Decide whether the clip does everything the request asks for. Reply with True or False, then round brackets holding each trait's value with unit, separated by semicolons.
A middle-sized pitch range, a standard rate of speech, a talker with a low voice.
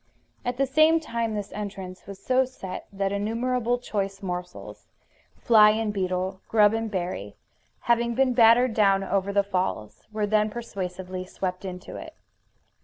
False (3.7 semitones; 150 wpm; 205 Hz)